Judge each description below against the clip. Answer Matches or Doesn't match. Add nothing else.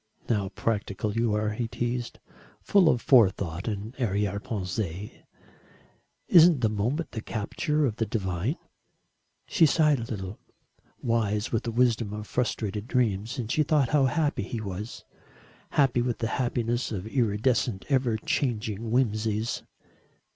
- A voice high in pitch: Doesn't match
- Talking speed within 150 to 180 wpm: Doesn't match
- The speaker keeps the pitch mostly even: Doesn't match